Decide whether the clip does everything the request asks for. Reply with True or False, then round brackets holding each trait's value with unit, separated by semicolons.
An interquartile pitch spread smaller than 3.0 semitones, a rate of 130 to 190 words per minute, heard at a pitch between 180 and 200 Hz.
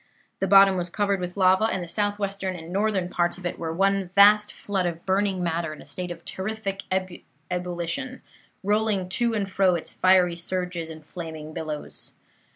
True (2.5 semitones; 175 wpm; 185 Hz)